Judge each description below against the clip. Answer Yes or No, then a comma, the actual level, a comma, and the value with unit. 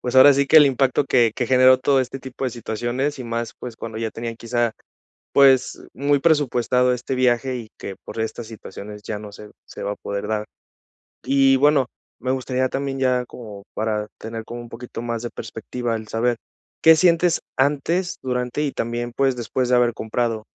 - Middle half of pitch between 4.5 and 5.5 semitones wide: No, average, 2.8 semitones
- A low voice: Yes, low, 125 Hz